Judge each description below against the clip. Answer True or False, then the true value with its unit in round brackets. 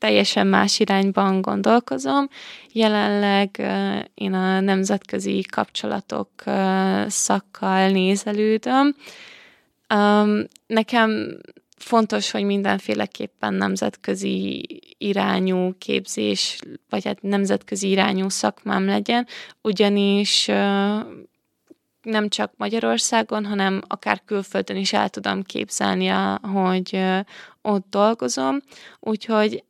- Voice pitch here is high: True (200 Hz)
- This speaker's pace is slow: True (75 wpm)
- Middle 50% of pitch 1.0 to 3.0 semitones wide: True (2.5 semitones)